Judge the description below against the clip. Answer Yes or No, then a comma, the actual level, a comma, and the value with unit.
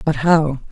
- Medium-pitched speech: Yes, medium, 150 Hz